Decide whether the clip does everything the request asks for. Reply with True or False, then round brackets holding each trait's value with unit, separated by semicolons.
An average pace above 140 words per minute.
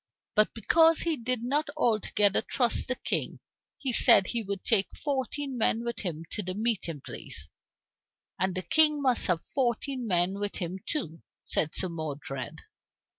True (160 wpm)